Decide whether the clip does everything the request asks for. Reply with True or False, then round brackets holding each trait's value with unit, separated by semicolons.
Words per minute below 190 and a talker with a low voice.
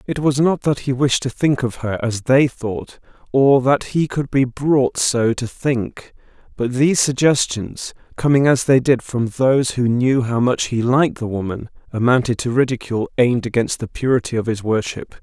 False (195 wpm; 125 Hz)